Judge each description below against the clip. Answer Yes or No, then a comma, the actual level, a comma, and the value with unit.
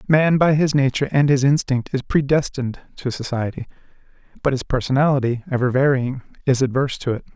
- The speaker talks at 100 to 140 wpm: No, average, 165 wpm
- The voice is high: No, low, 135 Hz